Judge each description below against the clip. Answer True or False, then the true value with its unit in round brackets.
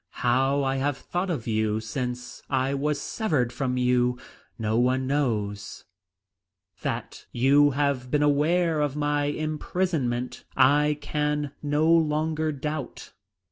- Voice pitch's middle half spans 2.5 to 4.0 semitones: True (3.2 semitones)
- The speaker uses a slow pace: True (125 wpm)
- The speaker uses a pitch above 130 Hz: True (140 Hz)